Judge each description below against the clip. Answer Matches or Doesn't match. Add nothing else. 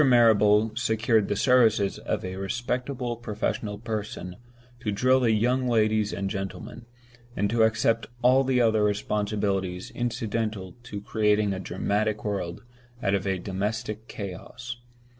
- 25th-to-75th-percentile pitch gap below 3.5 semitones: Matches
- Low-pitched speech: Matches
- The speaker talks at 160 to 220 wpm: Doesn't match